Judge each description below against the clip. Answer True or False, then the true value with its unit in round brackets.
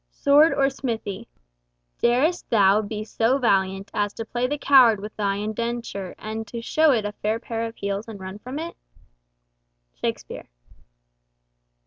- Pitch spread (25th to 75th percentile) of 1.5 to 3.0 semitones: False (3.5 semitones)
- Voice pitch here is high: True (225 Hz)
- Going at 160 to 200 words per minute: False (150 wpm)